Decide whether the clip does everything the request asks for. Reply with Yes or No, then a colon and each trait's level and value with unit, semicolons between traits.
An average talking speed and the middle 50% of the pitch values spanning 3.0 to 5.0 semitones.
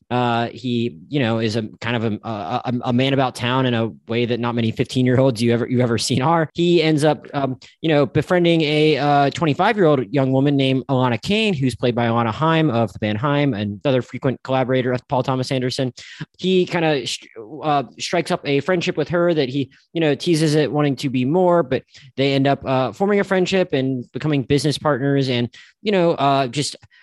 No: fast, 225 wpm; average, 3.7 semitones